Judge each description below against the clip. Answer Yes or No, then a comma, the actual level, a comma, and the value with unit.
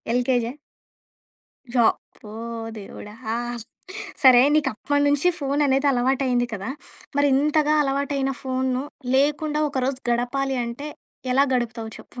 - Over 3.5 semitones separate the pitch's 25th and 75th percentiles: No, narrow, 2.6 semitones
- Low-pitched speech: No, very high, 265 Hz